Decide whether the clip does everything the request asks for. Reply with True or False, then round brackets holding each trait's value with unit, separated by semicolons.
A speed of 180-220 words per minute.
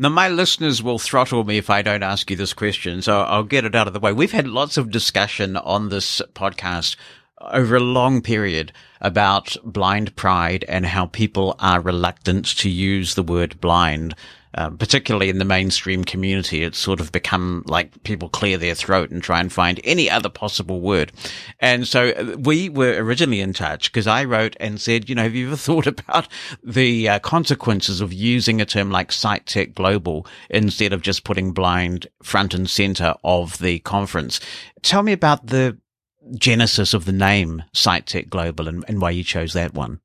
True (190 wpm)